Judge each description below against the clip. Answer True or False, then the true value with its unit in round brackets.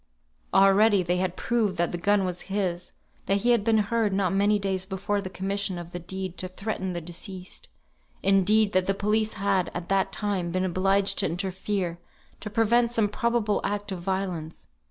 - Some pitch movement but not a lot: False (2.1 semitones)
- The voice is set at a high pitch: True (195 Hz)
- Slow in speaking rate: False (185 wpm)